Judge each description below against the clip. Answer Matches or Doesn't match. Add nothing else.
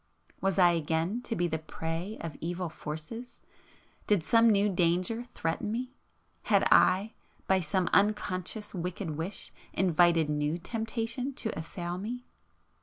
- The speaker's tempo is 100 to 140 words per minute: Matches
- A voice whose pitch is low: Doesn't match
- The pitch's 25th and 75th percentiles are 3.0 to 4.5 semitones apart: Doesn't match